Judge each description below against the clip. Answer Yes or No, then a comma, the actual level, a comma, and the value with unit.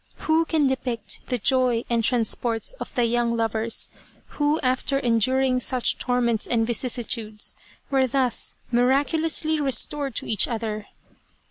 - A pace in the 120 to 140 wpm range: Yes, slow, 135 wpm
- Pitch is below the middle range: No, high, 245 Hz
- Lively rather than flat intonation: No, average, 2.8 semitones